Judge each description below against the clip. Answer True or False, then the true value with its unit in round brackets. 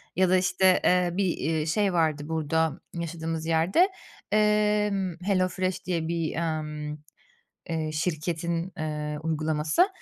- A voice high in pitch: False (165 Hz)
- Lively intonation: False (2.9 semitones)